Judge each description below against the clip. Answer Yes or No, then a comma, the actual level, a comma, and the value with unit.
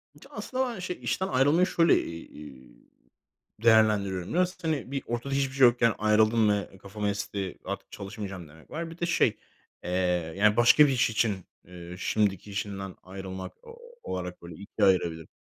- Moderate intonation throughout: No, wide, 6.2 semitones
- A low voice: Yes, low, 105 Hz